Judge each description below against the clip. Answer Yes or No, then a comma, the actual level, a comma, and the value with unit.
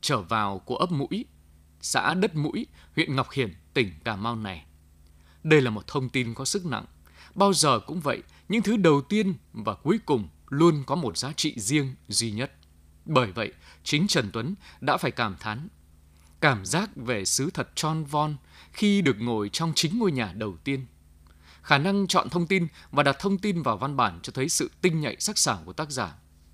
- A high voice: No, low, 135 Hz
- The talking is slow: No, average, 200 wpm